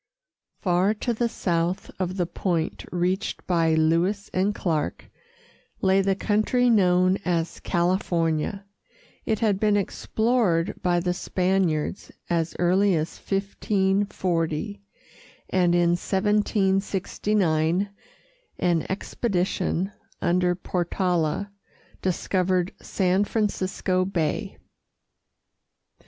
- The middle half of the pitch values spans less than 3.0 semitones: Yes, narrow, 2.5 semitones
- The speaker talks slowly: Yes, slow, 90 wpm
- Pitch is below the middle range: No, medium, 185 Hz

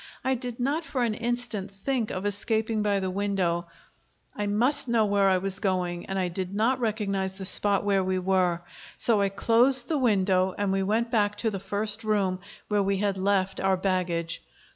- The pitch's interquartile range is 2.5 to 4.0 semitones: Yes, average, 2.9 semitones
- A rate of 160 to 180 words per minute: No, average, 195 wpm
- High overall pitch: Yes, high, 200 Hz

